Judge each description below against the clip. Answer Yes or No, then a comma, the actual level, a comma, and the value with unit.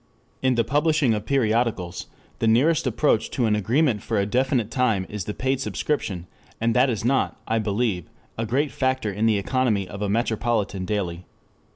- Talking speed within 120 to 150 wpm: No, average, 180 wpm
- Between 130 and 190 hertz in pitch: No, low, 115 Hz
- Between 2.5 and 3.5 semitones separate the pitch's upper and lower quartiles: No, average, 3.9 semitones